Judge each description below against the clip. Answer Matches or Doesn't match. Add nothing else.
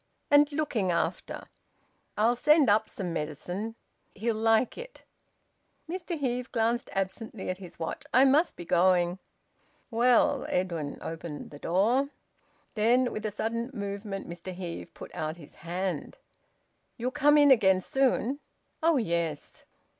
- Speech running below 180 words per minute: Matches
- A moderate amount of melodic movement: Doesn't match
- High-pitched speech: Matches